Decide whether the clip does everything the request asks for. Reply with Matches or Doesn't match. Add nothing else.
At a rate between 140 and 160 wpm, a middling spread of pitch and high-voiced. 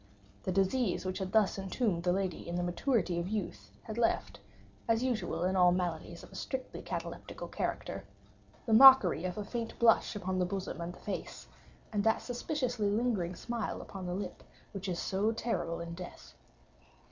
Doesn't match